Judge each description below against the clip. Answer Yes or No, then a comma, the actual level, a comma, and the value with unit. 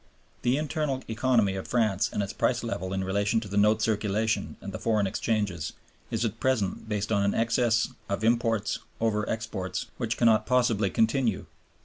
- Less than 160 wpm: No, average, 170 wpm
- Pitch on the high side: No, low, 110 Hz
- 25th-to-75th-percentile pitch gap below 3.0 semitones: Yes, narrow, 2.5 semitones